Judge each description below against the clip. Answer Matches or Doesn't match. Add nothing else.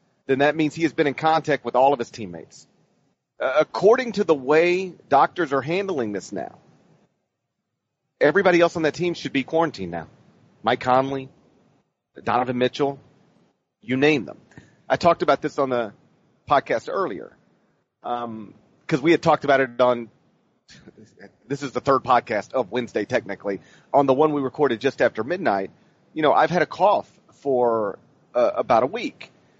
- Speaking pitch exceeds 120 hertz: Matches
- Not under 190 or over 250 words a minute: Doesn't match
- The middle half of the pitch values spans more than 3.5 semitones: Matches